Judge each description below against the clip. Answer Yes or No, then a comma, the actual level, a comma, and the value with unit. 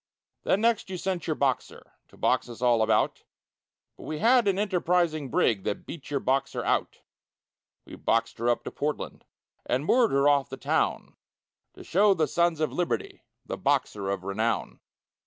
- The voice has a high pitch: No, medium, 150 Hz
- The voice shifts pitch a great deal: Yes, wide, 7.0 semitones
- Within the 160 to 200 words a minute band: Yes, average, 175 wpm